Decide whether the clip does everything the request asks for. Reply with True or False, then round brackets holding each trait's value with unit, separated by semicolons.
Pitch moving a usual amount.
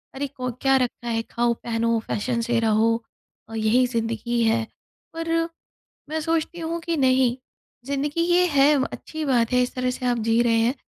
True (4.0 semitones)